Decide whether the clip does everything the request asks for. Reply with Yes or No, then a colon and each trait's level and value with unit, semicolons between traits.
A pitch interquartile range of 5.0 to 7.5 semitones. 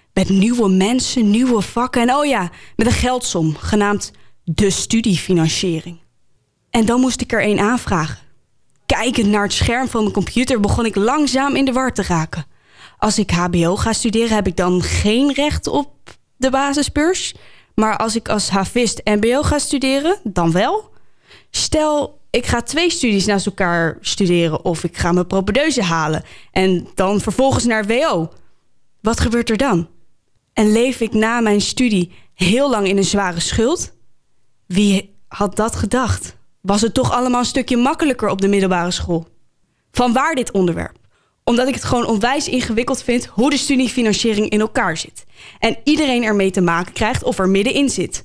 Yes: wide, 5.4 semitones